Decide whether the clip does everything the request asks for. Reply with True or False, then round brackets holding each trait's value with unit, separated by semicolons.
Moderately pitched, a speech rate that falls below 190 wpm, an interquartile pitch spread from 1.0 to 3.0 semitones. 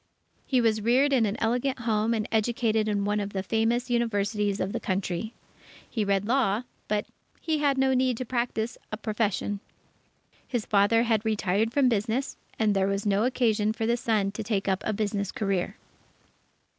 False (220 Hz; 180 wpm; 2.7 semitones)